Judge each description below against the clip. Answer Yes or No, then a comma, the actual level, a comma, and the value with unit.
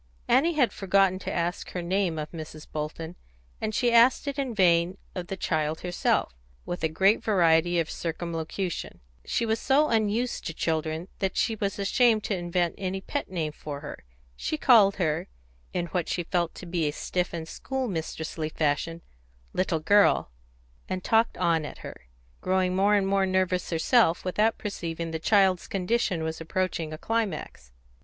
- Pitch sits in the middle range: Yes, medium, 180 Hz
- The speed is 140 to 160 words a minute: No, average, 175 wpm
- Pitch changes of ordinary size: Yes, average, 3.8 semitones